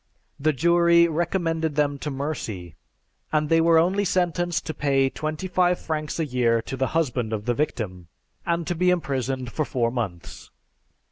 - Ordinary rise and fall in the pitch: Yes, average, 5.0 semitones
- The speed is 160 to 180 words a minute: Yes, average, 165 wpm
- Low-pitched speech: No, medium, 155 Hz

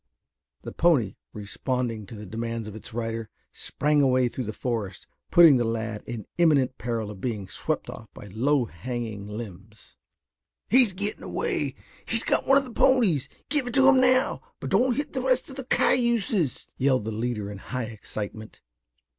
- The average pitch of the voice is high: No, low, 125 Hz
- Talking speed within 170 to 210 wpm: Yes, average, 175 wpm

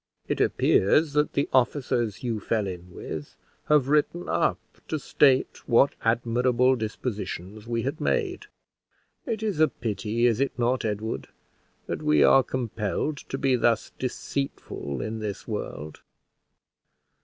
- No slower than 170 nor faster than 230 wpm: No, slow, 135 wpm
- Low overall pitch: Yes, low, 120 Hz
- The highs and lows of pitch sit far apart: No, average, 4.4 semitones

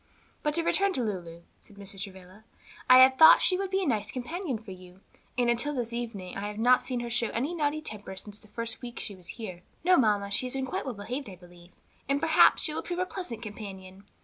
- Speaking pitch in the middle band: No, high, 230 Hz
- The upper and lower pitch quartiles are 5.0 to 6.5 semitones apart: Yes, wide, 5.4 semitones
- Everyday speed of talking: No, fast, 240 wpm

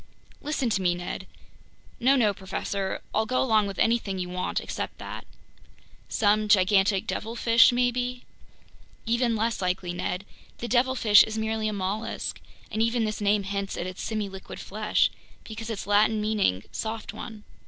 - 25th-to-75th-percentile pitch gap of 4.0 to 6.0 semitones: No, average, 2.8 semitones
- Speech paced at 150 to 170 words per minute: Yes, average, 155 wpm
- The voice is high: Yes, high, 215 Hz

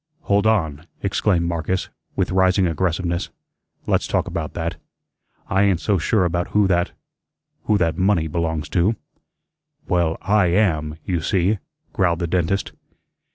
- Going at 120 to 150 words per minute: Yes, average, 140 wpm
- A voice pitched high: No, very low, 90 Hz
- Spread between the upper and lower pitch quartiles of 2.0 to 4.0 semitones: Yes, average, 2.8 semitones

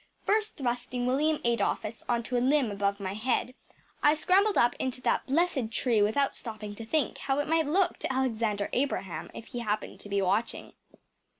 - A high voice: Yes, high, 245 Hz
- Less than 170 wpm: No, average, 185 wpm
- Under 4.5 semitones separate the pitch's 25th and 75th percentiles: No, average, 4.8 semitones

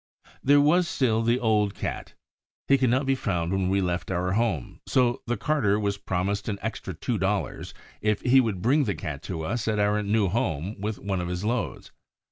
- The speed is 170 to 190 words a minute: No, fast, 205 wpm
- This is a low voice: Yes, low, 105 Hz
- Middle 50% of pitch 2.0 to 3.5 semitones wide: No, average, 4.1 semitones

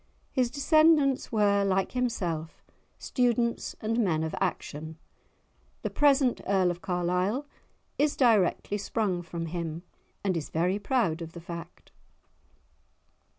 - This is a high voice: Yes, high, 195 Hz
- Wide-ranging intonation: Yes, wide, 6.2 semitones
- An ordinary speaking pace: No, slow, 120 wpm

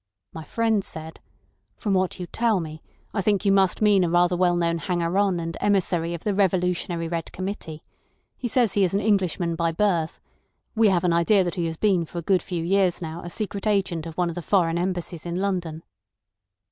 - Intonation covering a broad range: No, average, 2.8 semitones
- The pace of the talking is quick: Yes, fast, 210 wpm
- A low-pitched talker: No, medium, 180 Hz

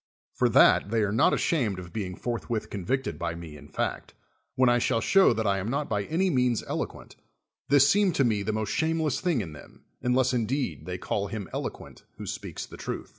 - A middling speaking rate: No, fast, 220 wpm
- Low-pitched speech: Yes, low, 115 Hz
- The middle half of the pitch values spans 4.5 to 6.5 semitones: Yes, average, 5.2 semitones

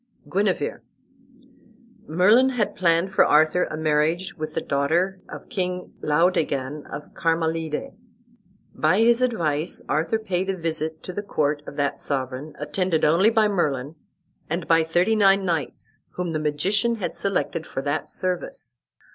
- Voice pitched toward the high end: No, medium, 165 Hz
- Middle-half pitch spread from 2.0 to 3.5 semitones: No, average, 4.0 semitones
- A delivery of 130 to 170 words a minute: Yes, average, 145 wpm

